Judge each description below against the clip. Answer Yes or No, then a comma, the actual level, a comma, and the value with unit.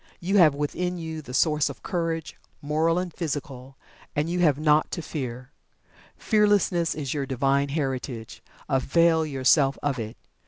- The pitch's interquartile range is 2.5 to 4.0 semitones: Yes, average, 3.5 semitones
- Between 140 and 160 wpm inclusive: Yes, average, 150 wpm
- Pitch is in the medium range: Yes, medium, 150 Hz